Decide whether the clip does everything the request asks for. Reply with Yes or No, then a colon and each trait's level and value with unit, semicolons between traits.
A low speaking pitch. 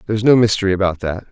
Yes: low, 100 Hz